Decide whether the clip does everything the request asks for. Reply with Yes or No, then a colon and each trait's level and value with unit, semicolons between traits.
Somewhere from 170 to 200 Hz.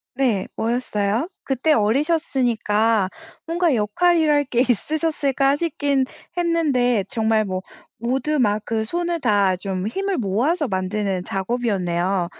No: high, 240 Hz